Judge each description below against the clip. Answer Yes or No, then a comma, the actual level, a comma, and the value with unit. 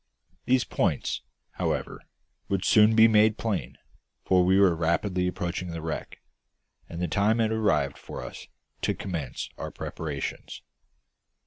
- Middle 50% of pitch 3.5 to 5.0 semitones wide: Yes, average, 4.4 semitones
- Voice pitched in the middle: No, very low, 95 Hz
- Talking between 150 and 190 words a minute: No, slow, 135 wpm